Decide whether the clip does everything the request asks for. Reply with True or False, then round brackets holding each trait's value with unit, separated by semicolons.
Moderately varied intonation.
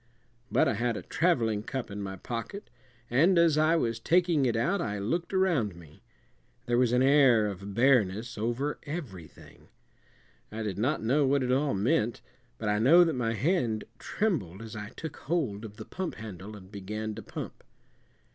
False (6.0 semitones)